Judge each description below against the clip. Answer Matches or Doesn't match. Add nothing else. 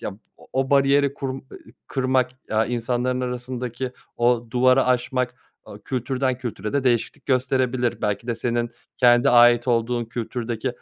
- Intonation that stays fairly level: Matches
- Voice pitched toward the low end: Matches